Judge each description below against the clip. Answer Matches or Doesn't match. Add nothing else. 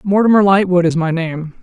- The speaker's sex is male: Doesn't match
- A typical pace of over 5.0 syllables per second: Matches